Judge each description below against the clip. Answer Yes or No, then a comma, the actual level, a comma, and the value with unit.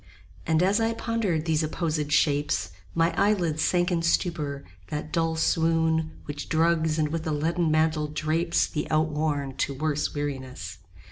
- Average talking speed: Yes, average, 155 wpm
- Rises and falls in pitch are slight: Yes, narrow, 1.9 semitones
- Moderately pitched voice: Yes, medium, 160 Hz